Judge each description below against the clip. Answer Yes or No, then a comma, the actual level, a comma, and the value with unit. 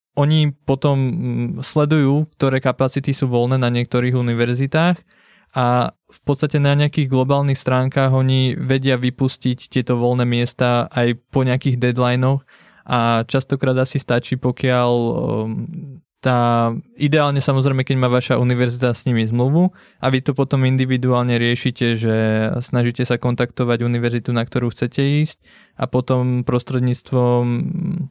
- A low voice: Yes, low, 130 Hz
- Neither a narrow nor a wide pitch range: No, narrow, 2.2 semitones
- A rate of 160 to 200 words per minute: No, average, 130 wpm